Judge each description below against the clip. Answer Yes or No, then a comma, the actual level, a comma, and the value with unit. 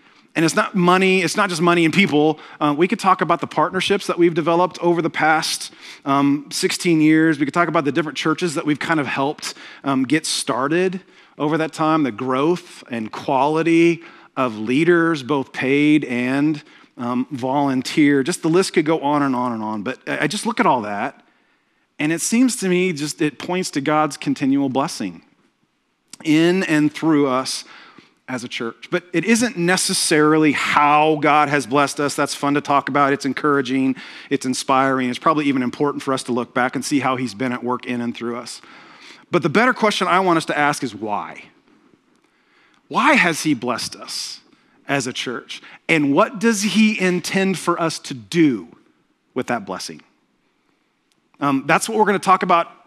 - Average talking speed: Yes, average, 190 wpm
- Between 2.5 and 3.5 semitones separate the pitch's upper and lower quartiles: No, average, 4.5 semitones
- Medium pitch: Yes, medium, 155 Hz